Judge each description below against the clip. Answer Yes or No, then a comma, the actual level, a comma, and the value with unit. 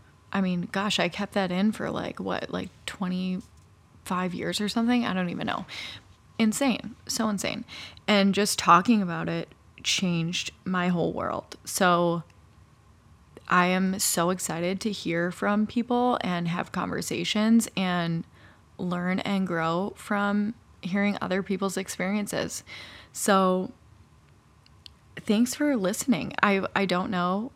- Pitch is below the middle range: No, medium, 185 Hz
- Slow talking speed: Yes, slow, 130 wpm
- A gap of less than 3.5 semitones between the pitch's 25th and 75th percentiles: Yes, average, 2.8 semitones